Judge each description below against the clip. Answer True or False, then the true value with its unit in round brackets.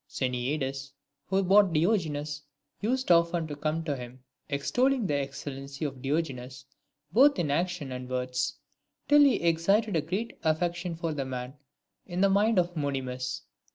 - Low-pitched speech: False (155 Hz)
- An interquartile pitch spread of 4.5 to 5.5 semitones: True (5.0 semitones)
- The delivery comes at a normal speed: True (150 wpm)